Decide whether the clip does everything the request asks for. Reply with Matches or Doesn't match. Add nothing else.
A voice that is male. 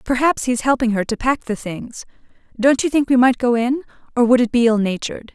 Doesn't match